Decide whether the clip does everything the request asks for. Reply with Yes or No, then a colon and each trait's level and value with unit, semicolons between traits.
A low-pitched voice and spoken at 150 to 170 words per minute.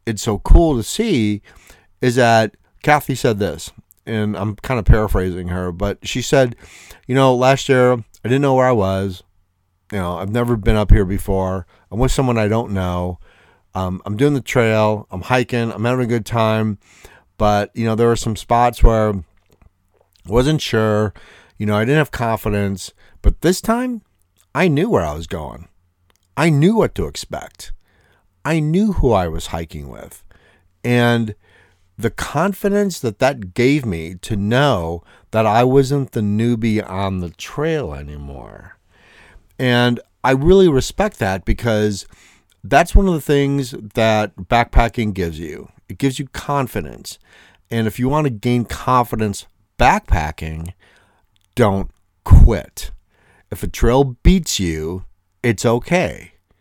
Yes: low, 105 Hz; average, 155 wpm